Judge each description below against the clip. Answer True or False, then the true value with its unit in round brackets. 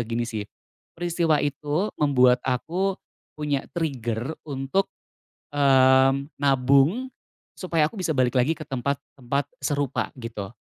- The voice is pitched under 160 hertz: True (140 Hz)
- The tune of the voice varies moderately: True (3.8 semitones)